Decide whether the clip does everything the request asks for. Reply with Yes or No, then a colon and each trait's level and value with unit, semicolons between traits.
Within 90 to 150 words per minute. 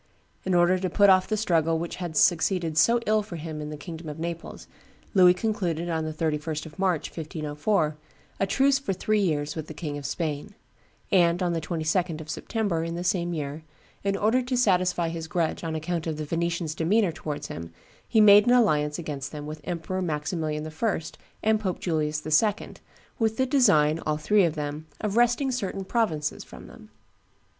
No: average, 190 wpm